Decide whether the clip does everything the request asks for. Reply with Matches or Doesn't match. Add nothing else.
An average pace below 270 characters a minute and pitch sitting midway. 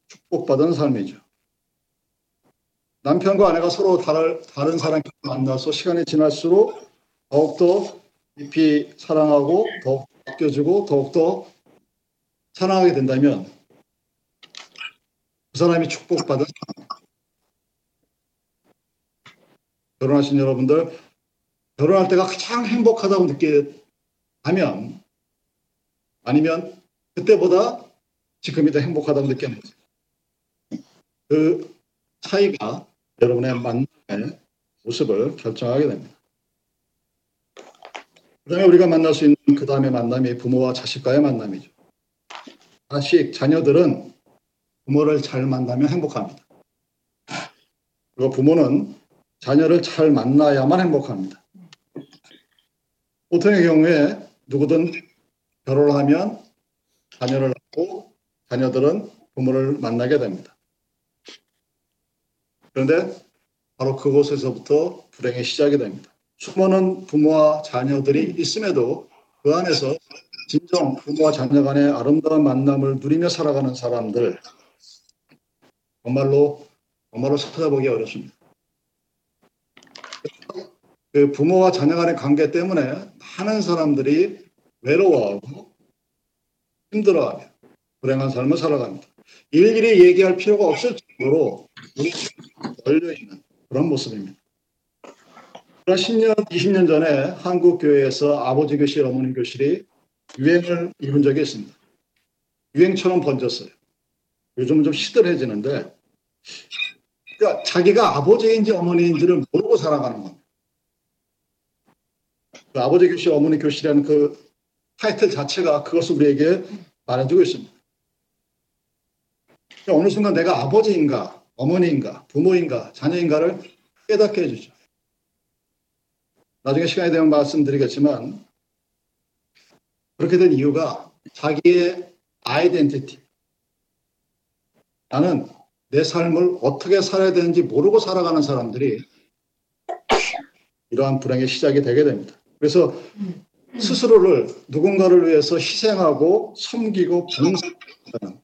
Matches